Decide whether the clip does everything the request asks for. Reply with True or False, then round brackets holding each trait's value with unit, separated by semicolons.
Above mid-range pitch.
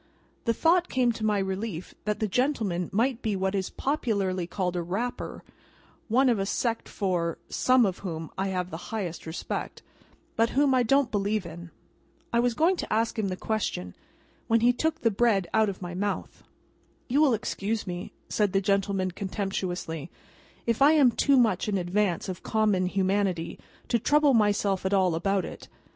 True (205 Hz)